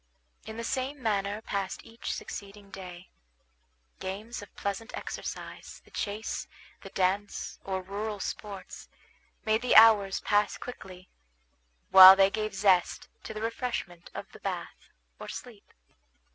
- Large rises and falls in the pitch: No, narrow, 2.4 semitones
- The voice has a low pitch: No, high, 205 Hz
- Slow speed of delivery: Yes, slow, 130 wpm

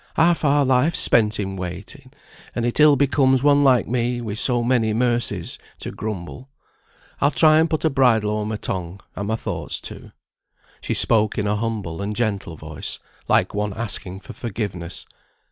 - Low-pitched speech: Yes, low, 115 Hz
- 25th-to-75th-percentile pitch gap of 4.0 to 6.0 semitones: Yes, average, 4.4 semitones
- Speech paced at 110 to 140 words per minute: No, average, 170 wpm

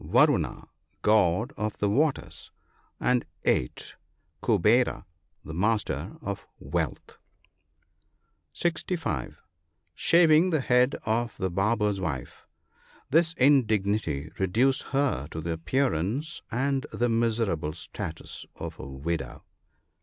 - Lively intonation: Yes, wide, 7.9 semitones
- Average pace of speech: No, slow, 105 wpm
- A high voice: No, low, 110 Hz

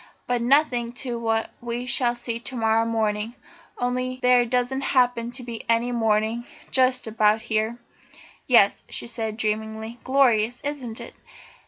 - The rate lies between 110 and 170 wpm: Yes, average, 145 wpm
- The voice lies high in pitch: Yes, high, 235 Hz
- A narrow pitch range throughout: Yes, narrow, 1.9 semitones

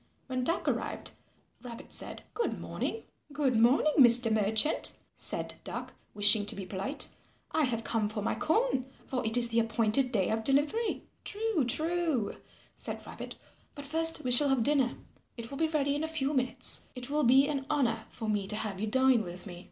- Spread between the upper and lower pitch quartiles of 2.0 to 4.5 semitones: No, average, 4.9 semitones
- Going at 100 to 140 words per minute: No, average, 190 wpm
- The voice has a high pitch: Yes, very high, 255 Hz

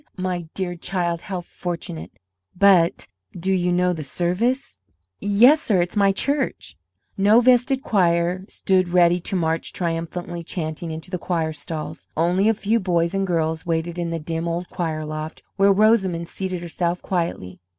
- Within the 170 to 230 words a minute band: No, average, 160 wpm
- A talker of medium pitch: Yes, medium, 175 Hz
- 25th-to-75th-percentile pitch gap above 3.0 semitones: No, narrow, 2.5 semitones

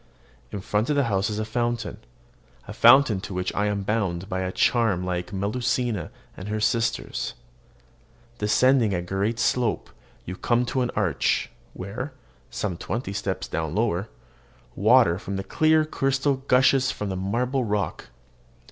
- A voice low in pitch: Yes, low, 105 Hz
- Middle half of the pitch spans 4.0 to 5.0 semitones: Yes, average, 4.3 semitones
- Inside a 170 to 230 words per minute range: No, average, 155 wpm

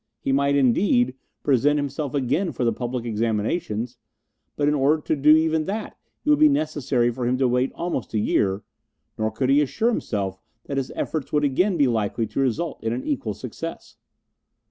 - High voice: No, low, 135 Hz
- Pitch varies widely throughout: No, average, 4.7 semitones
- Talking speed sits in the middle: Yes, average, 190 wpm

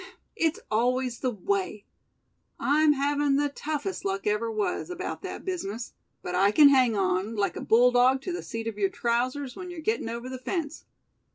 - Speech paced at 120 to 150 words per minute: No, average, 180 wpm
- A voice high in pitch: Yes, very high, 250 Hz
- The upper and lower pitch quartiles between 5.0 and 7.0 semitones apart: Yes, average, 5.3 semitones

